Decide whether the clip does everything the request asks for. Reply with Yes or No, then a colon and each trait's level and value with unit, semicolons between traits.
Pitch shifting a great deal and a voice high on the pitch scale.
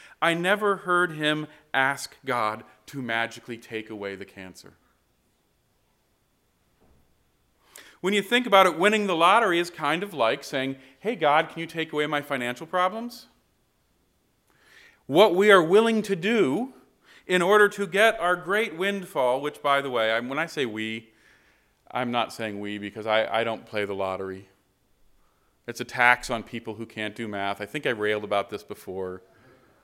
No: wide, 8.9 semitones; low, 130 Hz